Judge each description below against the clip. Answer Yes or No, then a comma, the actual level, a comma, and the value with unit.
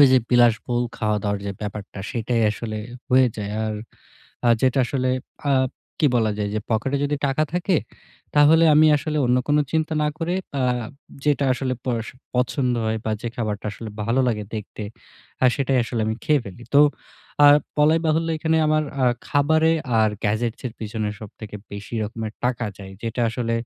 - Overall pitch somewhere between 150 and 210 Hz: No, low, 120 Hz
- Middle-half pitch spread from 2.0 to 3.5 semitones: No, average, 4.9 semitones